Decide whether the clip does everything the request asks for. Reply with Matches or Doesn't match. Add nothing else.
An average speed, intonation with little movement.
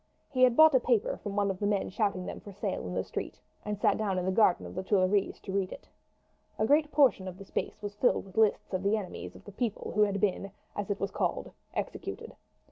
Doesn't match